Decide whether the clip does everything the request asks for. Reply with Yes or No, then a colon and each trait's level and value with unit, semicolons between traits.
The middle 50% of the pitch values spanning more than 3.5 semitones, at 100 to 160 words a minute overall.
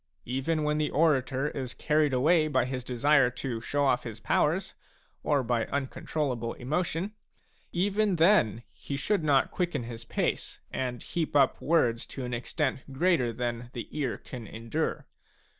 Yes: average, 4.1 semitones; average, 155 wpm